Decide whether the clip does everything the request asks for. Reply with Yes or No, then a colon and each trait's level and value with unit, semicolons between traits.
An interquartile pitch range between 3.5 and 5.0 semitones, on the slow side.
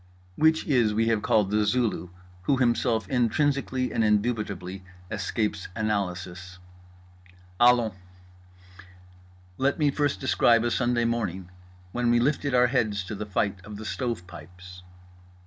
Yes: average, 4.2 semitones; slow, 130 wpm